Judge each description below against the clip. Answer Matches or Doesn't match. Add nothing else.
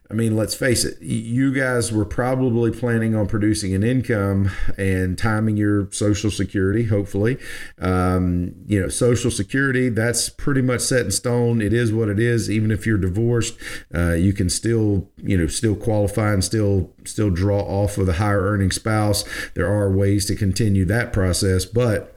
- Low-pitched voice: Matches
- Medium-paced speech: Matches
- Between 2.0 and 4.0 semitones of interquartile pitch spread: Matches